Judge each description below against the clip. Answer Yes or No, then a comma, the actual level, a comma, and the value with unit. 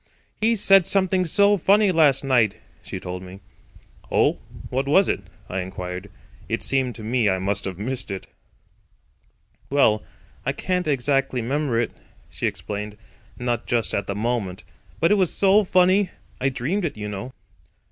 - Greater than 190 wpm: No, average, 160 wpm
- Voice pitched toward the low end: Yes, low, 130 Hz